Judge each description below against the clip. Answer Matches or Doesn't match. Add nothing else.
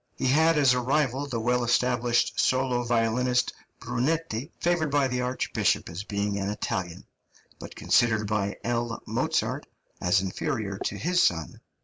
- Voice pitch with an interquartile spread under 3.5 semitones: Doesn't match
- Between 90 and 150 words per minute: Matches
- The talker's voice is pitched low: Matches